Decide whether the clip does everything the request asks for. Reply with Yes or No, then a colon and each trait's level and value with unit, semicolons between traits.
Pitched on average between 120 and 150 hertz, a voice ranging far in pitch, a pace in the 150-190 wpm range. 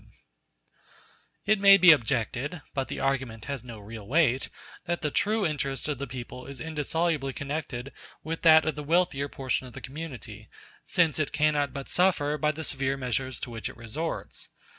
No: medium, 140 Hz; average, 3.7 semitones; average, 180 wpm